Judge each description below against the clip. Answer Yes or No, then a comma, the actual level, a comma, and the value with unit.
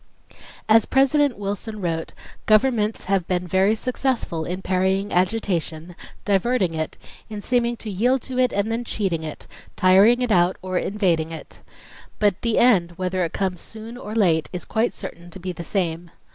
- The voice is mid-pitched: No, high, 195 Hz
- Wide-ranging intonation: No, average, 4.2 semitones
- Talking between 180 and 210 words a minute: No, average, 170 wpm